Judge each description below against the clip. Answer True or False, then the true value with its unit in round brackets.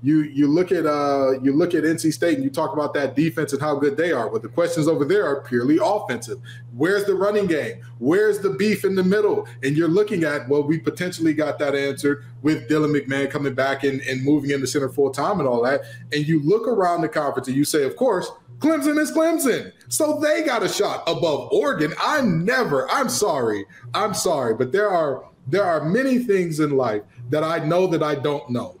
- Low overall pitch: False (150 Hz)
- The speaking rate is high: True (225 wpm)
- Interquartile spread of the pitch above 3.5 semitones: True (4.3 semitones)